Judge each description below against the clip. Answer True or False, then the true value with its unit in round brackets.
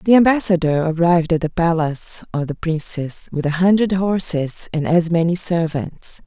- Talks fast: False (165 wpm)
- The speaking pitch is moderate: True (170 Hz)